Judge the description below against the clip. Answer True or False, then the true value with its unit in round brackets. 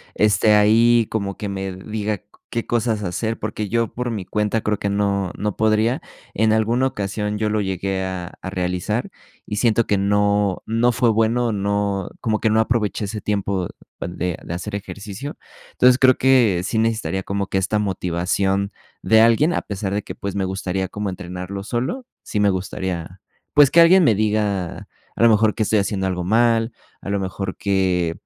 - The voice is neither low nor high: False (105 Hz)